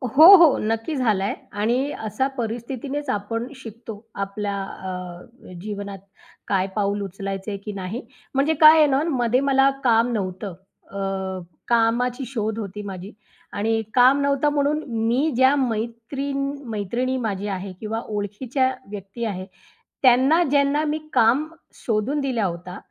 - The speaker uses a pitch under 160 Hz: No, high, 225 Hz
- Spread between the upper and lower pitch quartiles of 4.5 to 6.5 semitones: Yes, average, 4.8 semitones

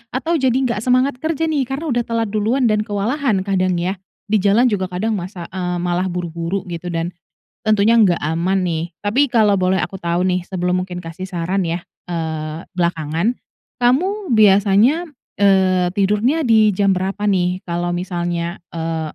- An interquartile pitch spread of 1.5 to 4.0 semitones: No, average, 4.4 semitones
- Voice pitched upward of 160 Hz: Yes, high, 190 Hz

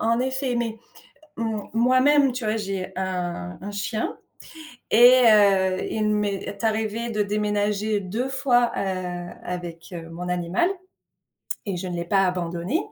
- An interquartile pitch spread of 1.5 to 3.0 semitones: No, average, 4.1 semitones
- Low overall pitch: No, high, 205 Hz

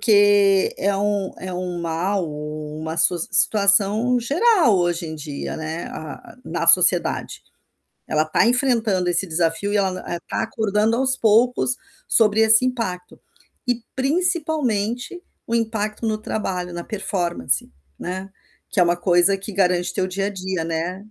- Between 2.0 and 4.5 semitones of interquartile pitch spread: Yes, average, 4.2 semitones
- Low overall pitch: No, high, 195 Hz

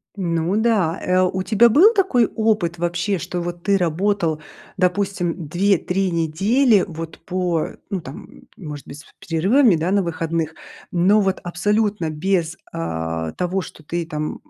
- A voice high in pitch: No, medium, 175 Hz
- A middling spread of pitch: Yes, average, 3.6 semitones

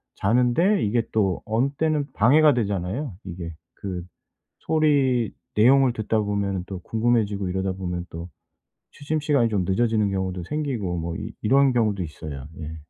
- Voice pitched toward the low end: Yes, low, 105 Hz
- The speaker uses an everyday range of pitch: No, wide, 5.8 semitones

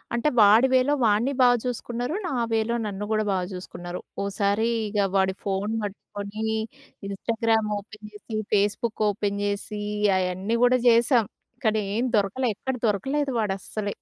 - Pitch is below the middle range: No, high, 215 Hz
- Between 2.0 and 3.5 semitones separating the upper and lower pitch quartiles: Yes, average, 2.7 semitones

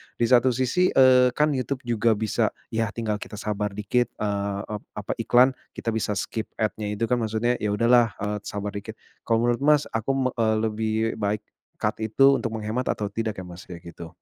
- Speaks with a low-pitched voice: Yes, low, 110 Hz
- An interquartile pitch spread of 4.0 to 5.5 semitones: No, average, 2.8 semitones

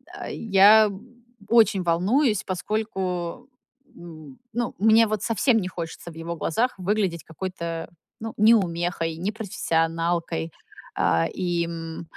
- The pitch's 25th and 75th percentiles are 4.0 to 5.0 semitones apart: Yes, average, 4.5 semitones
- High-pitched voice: No, medium, 180 Hz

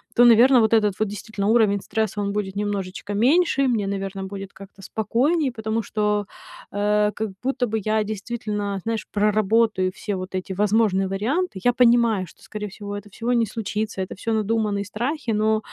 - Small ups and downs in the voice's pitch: Yes, narrow, 2.2 semitones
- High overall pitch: Yes, high, 210 Hz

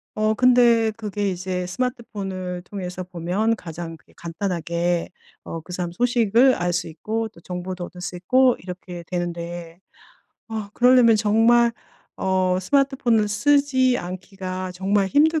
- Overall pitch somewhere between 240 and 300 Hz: No, high, 190 Hz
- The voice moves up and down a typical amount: Yes, average, 4.4 semitones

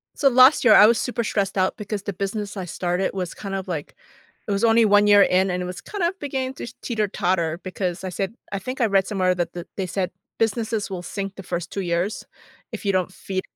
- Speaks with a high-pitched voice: Yes, high, 195 Hz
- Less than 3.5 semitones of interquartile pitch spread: Yes, average, 3.0 semitones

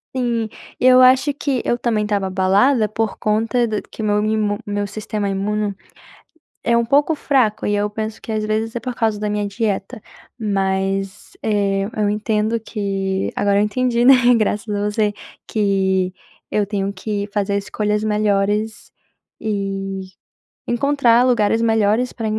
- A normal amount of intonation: No, narrow, 2.1 semitones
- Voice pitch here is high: Yes, high, 210 Hz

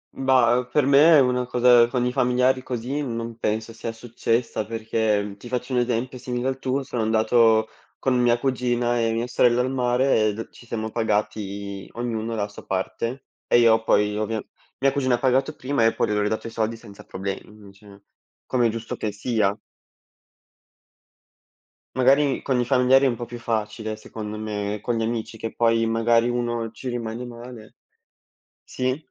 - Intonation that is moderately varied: No, narrow, 2.3 semitones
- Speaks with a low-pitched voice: Yes, low, 115 Hz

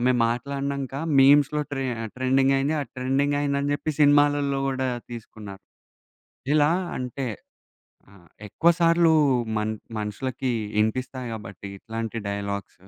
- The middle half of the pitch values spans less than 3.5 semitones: No, average, 4.0 semitones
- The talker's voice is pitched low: Yes, low, 130 Hz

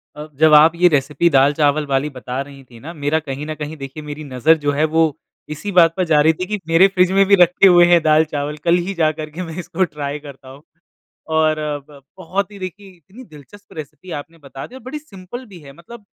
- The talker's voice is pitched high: No, medium, 155 Hz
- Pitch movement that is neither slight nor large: Yes, average, 3.9 semitones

